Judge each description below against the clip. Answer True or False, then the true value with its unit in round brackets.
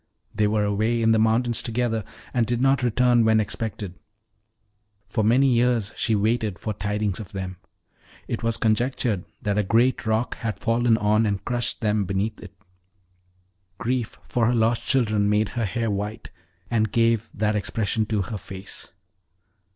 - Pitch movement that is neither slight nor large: False (2.2 semitones)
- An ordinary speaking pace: True (160 wpm)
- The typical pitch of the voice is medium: False (110 Hz)